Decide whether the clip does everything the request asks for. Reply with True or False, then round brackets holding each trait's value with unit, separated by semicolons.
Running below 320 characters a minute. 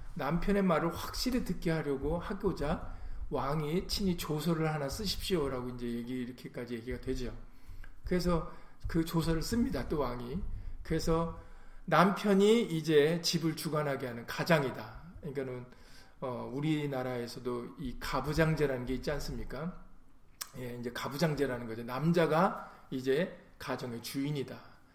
True (310 characters per minute)